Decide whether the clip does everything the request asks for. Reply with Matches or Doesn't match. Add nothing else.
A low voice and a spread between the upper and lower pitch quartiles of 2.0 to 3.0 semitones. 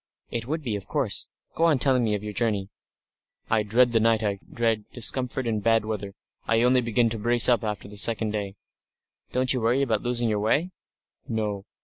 Matches